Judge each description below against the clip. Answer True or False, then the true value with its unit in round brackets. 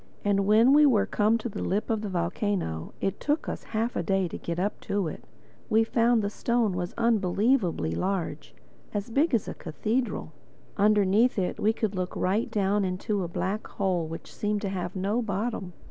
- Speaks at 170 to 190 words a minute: True (185 wpm)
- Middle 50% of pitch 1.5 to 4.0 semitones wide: True (3.4 semitones)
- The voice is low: False (205 Hz)